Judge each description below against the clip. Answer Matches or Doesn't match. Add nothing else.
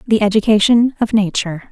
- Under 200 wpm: Matches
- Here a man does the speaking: Doesn't match